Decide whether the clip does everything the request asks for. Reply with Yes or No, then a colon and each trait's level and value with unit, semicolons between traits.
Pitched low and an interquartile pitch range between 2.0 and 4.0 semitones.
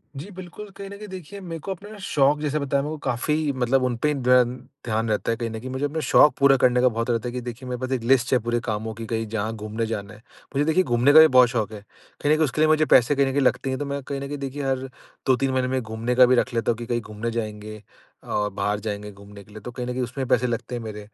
Yes: low, 125 Hz; average, 3.7 semitones